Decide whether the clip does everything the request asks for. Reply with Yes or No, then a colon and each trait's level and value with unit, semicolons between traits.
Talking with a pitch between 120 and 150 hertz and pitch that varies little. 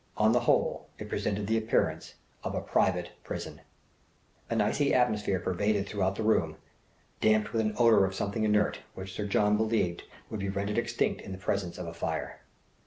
No: low, 105 Hz; narrow, 2.1 semitones